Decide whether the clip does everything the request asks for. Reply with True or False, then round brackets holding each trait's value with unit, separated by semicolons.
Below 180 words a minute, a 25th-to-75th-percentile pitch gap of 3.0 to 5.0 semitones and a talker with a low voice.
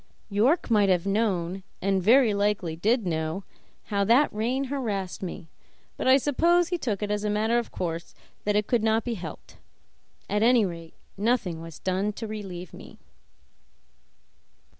False (160 wpm; 4.1 semitones; 210 Hz)